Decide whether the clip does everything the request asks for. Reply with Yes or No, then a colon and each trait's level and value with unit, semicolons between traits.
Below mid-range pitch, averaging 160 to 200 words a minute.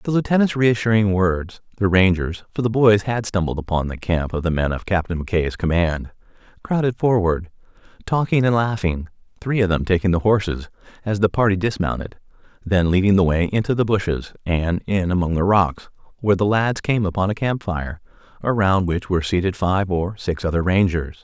Yes: very low, 95 Hz; average, 180 wpm